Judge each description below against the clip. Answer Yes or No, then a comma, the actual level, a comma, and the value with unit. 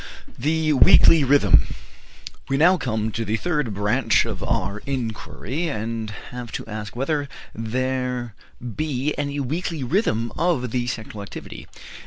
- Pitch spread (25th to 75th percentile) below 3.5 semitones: No, average, 4.6 semitones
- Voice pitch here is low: Yes, low, 125 Hz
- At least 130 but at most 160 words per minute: Yes, slow, 135 wpm